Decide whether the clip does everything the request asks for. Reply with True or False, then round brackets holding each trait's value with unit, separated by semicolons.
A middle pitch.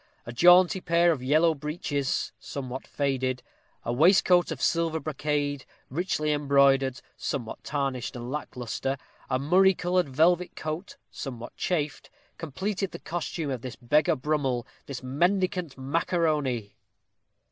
True (145 Hz)